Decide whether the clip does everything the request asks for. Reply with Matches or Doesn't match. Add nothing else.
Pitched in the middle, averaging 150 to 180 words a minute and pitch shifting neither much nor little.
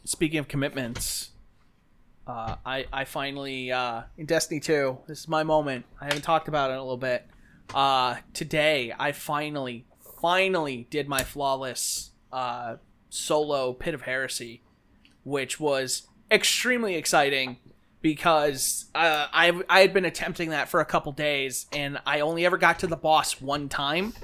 Matches